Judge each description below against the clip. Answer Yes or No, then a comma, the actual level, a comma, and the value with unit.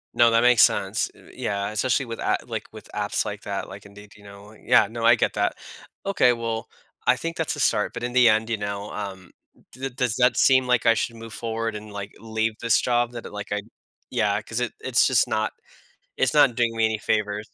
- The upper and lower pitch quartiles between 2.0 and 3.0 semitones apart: Yes, average, 2.7 semitones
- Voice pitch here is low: Yes, low, 115 Hz